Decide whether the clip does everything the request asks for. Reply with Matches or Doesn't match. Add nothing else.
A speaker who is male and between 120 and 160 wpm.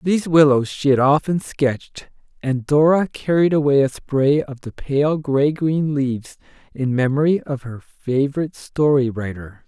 Matches